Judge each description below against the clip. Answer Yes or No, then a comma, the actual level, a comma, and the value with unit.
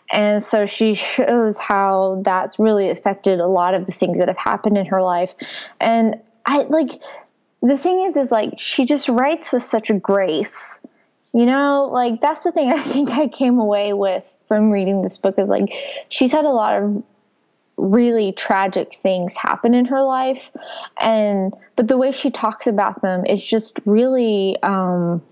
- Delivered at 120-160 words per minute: No, average, 180 wpm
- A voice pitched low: No, high, 220 Hz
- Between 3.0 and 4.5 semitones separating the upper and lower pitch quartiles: No, average, 5.3 semitones